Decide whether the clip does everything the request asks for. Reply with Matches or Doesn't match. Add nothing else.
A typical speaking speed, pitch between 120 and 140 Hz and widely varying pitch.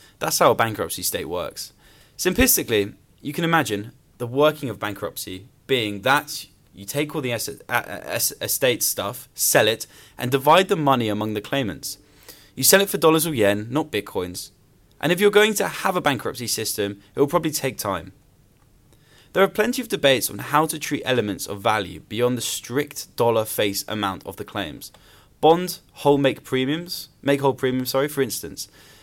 Matches